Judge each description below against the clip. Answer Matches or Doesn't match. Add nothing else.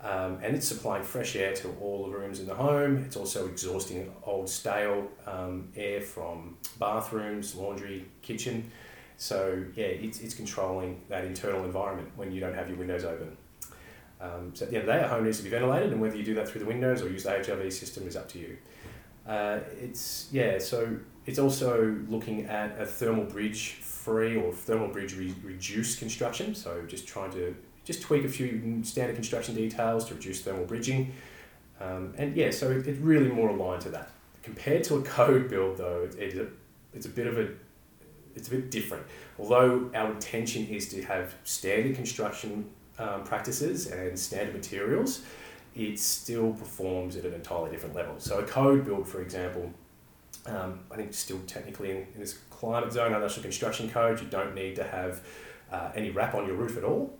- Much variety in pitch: Doesn't match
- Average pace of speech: Matches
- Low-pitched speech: Matches